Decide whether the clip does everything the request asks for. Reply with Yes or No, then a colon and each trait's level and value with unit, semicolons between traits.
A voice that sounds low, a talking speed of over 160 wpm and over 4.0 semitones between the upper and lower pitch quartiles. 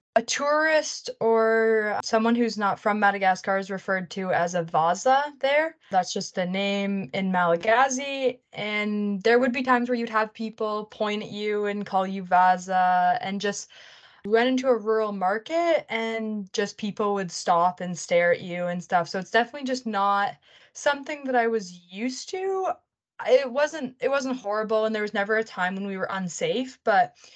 No: high, 210 Hz; average, 180 wpm; average, 4.6 semitones